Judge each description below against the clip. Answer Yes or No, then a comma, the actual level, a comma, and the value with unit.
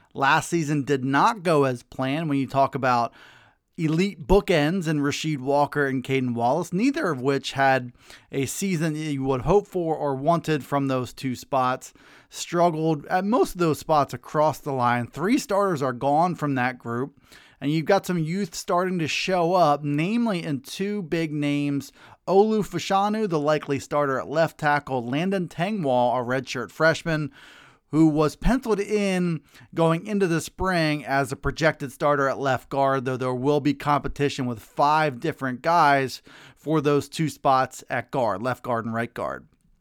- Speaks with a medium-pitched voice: Yes, medium, 145 Hz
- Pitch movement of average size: Yes, average, 4.0 semitones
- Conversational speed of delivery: Yes, average, 170 wpm